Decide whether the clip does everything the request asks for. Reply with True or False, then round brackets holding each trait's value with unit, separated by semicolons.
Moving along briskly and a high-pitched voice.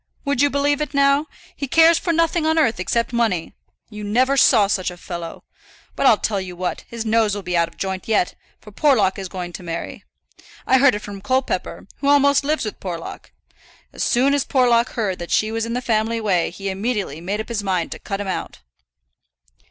True (215 wpm; 220 Hz)